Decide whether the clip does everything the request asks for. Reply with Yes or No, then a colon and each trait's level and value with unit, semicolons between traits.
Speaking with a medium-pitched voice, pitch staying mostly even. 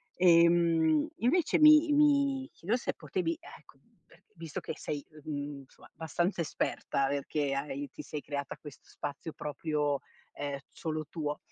No: medium, 155 Hz; average, 4.3 semitones